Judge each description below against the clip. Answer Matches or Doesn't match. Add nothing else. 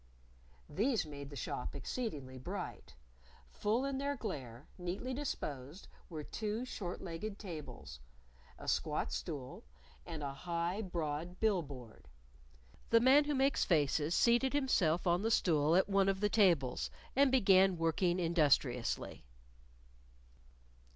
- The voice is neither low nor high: Matches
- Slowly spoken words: Matches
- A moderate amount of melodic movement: Doesn't match